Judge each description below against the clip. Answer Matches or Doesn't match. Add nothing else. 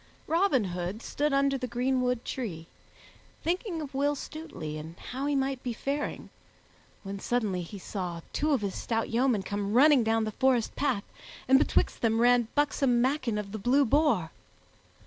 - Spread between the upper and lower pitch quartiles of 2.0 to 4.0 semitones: Doesn't match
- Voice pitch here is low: Doesn't match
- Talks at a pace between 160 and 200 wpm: Matches